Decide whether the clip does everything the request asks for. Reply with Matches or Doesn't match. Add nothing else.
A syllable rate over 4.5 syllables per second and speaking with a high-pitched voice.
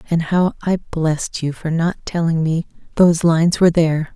Doesn't match